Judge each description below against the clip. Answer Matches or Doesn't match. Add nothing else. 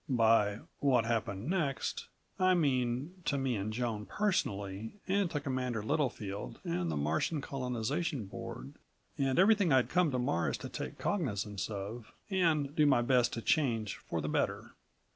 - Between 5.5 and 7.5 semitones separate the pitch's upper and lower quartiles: Matches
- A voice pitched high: Doesn't match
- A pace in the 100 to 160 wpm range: Matches